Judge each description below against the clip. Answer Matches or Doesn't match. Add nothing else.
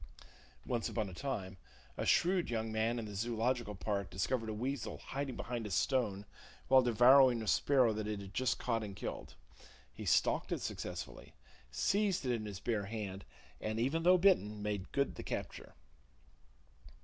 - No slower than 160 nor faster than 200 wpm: Matches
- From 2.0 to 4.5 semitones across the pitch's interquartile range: Matches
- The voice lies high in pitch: Doesn't match